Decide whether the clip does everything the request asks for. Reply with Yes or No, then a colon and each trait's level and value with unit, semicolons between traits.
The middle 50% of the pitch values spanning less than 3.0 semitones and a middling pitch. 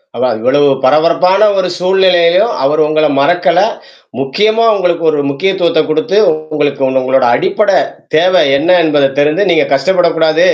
No: average, 3.8 semitones; medium, 165 Hz